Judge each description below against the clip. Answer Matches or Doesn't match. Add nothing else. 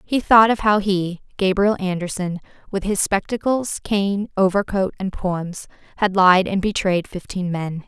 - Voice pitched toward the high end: Matches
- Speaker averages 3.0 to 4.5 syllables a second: Matches